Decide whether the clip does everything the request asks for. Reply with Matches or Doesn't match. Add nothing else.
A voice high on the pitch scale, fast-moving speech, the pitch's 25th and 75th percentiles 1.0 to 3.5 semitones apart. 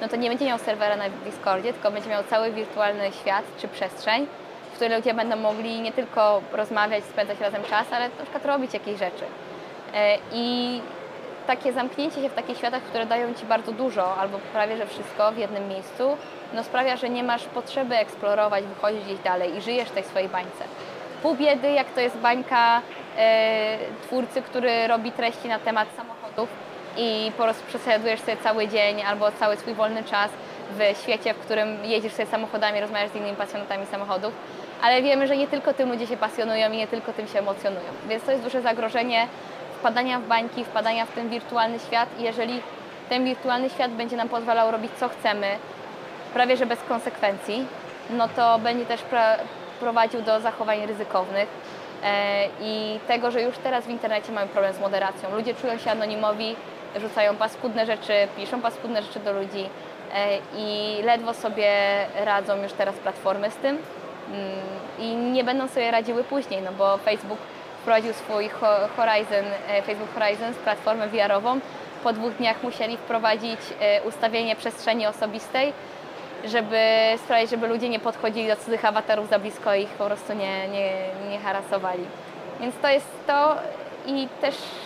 Matches